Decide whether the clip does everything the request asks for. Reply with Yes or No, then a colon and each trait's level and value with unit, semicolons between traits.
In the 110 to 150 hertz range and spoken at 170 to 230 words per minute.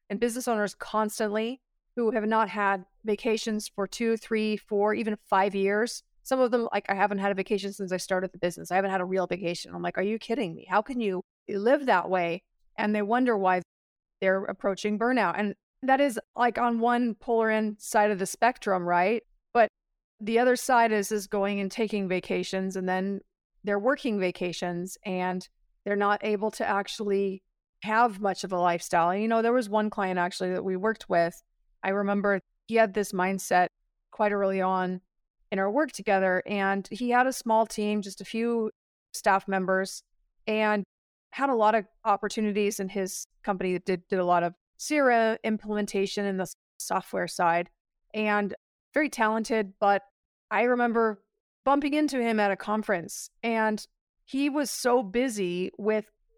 No: high, 210 Hz; average, 180 wpm